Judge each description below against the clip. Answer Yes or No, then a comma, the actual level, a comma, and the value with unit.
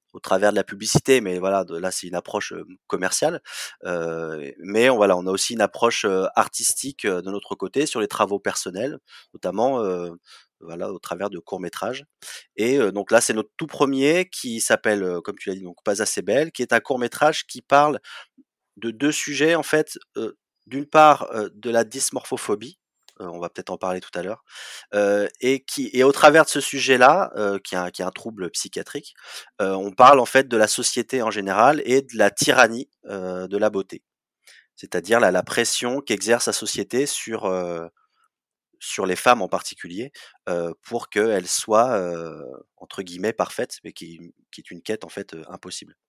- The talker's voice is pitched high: No, low, 110 Hz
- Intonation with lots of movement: Yes, wide, 6.5 semitones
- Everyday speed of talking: Yes, average, 195 wpm